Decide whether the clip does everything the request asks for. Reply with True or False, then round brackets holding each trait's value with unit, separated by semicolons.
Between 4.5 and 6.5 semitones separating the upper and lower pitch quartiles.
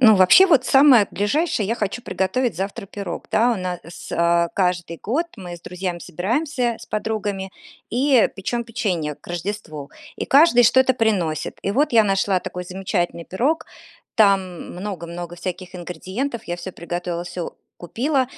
True (5.1 semitones)